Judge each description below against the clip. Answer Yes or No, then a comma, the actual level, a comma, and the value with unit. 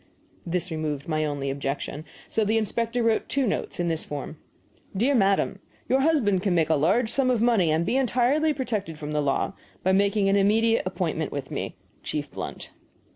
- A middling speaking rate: Yes, average, 185 wpm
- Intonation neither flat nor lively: No, wide, 6.7 semitones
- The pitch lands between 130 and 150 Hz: No, high, 195 Hz